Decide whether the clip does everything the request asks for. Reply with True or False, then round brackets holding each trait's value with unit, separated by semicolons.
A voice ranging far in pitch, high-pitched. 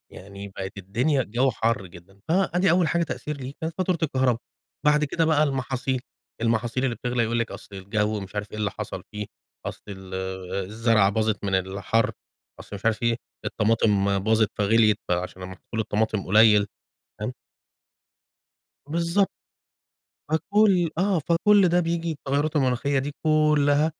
False (6.8 semitones; 120 Hz)